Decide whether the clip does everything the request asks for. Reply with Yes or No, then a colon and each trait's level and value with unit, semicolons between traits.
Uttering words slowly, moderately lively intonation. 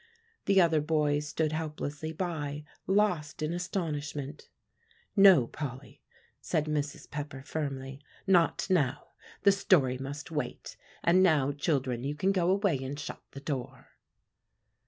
Yes: slow, 130 wpm; average, 3.3 semitones